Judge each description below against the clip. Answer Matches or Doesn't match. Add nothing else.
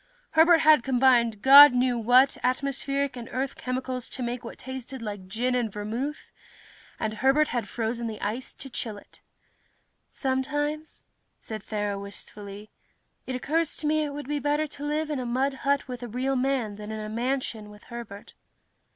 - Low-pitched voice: Doesn't match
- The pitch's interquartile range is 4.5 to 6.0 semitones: Doesn't match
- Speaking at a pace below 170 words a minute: Doesn't match